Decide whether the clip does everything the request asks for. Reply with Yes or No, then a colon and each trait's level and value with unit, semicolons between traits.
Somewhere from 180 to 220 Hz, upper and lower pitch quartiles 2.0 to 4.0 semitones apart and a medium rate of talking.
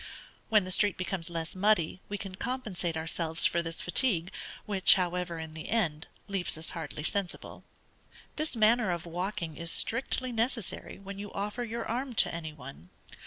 No: medium, 185 Hz; average, 4.5 semitones; average, 165 wpm